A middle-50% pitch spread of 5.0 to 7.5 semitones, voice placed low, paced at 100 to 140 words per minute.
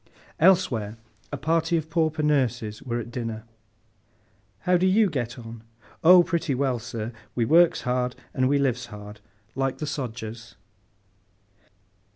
Yes: wide, 5.5 semitones; low, 130 Hz; slow, 135 wpm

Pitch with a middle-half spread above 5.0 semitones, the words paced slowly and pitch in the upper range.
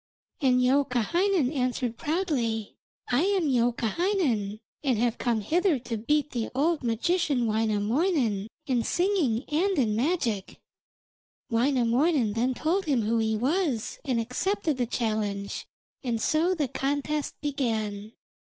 Yes: wide, 5.4 semitones; slow, 125 wpm; very high, 250 Hz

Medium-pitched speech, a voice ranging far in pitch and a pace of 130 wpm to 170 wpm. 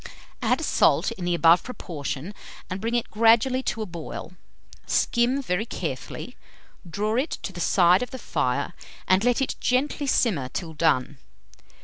No: high, 210 Hz; wide, 6.2 semitones; average, 155 wpm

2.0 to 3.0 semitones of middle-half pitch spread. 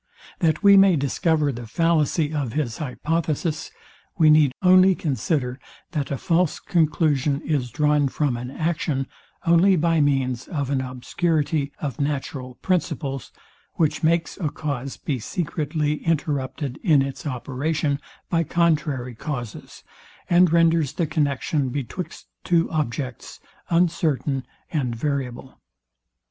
No: average, 3.6 semitones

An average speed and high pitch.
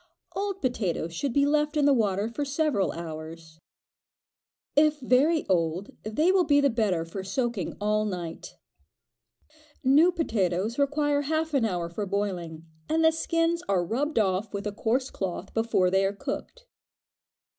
Yes: average, 155 wpm; high, 225 Hz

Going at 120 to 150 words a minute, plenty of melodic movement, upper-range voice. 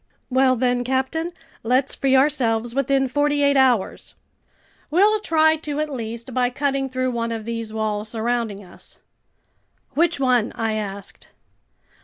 No: average, 140 wpm; average, 3.6 semitones; very high, 255 Hz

